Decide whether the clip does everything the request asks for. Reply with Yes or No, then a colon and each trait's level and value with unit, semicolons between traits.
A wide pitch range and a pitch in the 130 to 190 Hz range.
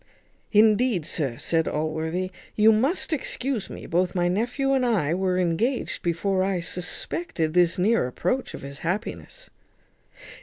Yes: wide, 5.7 semitones; medium, 185 Hz